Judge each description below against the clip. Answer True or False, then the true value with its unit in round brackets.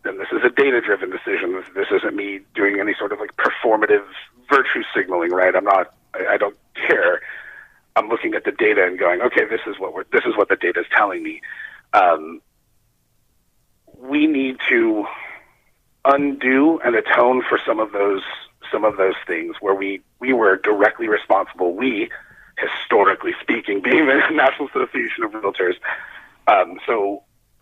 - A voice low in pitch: False (370 Hz)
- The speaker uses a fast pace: False (165 wpm)